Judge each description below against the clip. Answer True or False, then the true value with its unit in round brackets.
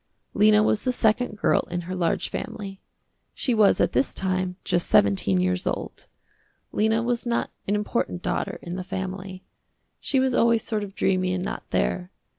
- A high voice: True (195 Hz)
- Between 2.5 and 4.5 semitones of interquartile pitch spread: True (3.2 semitones)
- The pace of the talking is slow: False (175 wpm)